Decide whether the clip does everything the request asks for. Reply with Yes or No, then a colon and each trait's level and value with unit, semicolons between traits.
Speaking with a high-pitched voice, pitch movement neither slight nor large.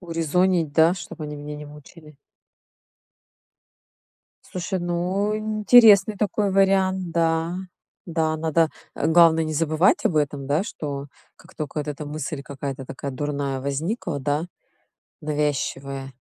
No: medium, 160 Hz; average, 3.6 semitones